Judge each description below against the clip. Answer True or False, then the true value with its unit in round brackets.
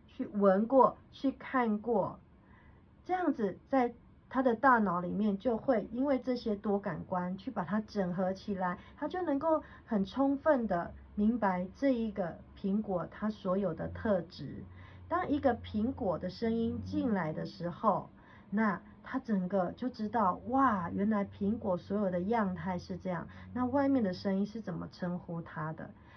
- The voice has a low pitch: False (210 Hz)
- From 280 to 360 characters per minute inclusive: False (225 characters per minute)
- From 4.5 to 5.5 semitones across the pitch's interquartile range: True (5.2 semitones)